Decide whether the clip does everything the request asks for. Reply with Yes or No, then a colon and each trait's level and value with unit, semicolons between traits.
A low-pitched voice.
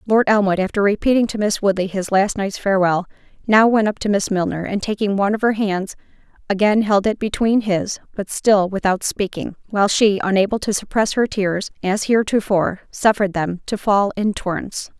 No: high, 200 Hz